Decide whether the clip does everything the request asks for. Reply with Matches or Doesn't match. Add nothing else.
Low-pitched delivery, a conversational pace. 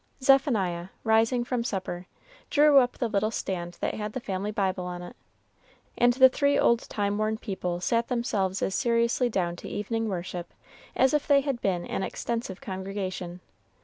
Doesn't match